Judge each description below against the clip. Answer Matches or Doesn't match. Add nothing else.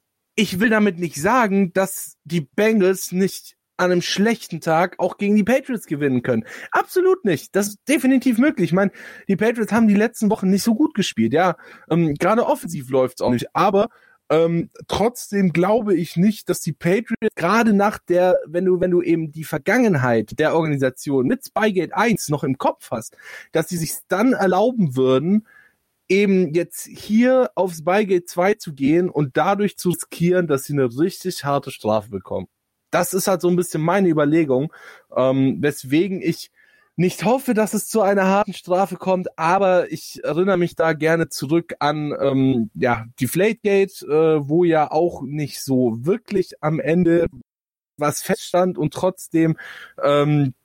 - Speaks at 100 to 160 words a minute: Doesn't match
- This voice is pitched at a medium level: Matches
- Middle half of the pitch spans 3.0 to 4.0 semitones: Doesn't match